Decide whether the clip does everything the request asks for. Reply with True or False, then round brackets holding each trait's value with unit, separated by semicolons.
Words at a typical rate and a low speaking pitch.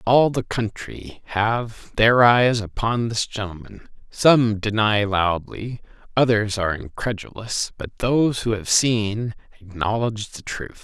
False (125 wpm; 110 Hz)